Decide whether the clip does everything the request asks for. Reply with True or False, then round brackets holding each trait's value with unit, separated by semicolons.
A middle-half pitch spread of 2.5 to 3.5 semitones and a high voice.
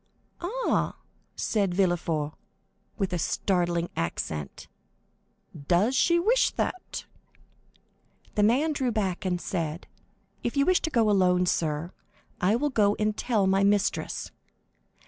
False (5.5 semitones; 200 Hz)